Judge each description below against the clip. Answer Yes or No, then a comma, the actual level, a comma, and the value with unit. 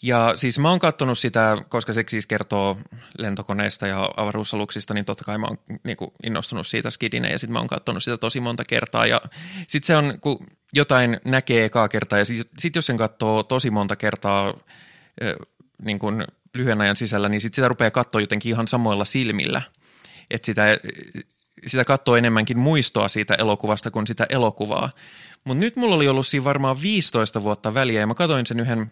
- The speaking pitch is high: No, low, 115 Hz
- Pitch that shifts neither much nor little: Yes, average, 3.6 semitones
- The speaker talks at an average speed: No, fast, 185 wpm